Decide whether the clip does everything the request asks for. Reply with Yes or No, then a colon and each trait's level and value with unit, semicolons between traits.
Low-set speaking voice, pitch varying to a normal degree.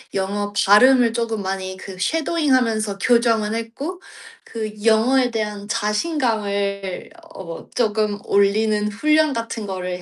No: high, 215 Hz; average, 3.0 semitones